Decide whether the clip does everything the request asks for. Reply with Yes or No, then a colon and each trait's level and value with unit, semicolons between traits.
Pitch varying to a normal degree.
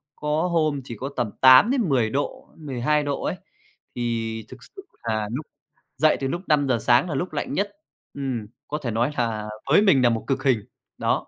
Yes: average, 4.2 semitones